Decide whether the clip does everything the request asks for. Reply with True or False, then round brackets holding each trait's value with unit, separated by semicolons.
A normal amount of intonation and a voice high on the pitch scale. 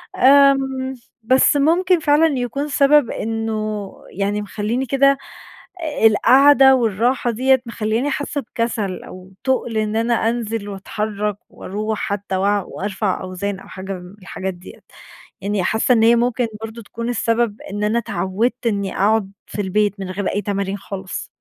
True (3.9 semitones; 220 Hz)